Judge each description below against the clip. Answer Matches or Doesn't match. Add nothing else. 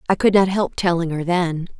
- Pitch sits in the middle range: Matches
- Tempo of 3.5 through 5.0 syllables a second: Doesn't match